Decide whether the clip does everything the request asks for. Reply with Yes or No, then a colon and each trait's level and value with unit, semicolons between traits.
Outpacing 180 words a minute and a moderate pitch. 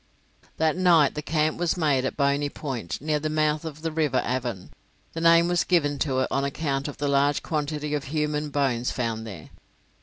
Yes: average, 200 wpm; medium, 145 Hz